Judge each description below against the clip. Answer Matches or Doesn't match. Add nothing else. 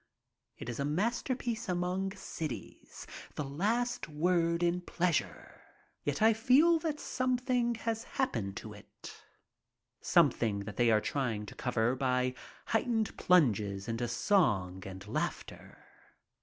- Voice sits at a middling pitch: Matches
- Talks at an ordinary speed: Doesn't match